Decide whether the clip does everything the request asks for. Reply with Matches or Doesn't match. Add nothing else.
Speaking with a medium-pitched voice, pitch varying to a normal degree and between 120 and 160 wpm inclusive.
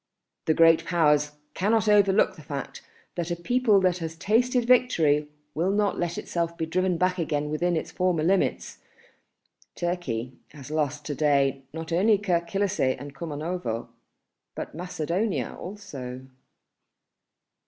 Matches